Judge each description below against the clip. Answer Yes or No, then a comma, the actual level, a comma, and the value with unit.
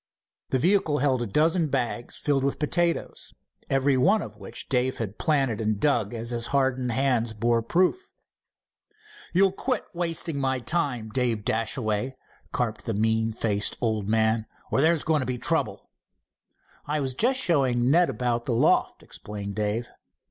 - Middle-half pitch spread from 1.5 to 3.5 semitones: No, average, 4.8 semitones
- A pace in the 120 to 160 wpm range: Yes, average, 155 wpm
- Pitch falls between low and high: No, low, 125 Hz